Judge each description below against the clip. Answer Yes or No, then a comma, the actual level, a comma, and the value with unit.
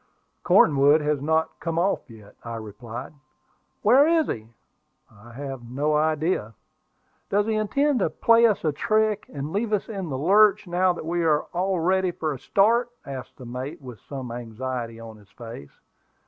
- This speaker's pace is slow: No, average, 175 wpm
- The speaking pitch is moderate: Yes, medium, 155 Hz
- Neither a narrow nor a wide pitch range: No, wide, 8.0 semitones